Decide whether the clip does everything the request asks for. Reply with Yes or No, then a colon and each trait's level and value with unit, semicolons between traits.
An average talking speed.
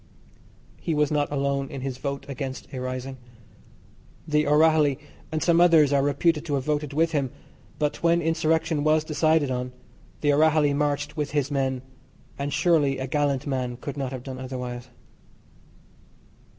Yes: average, 160 wpm